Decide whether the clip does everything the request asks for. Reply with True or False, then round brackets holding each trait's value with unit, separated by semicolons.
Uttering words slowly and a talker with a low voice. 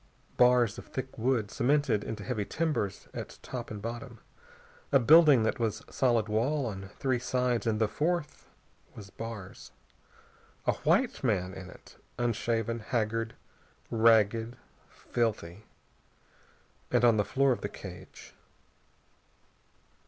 True (125 wpm; 115 Hz)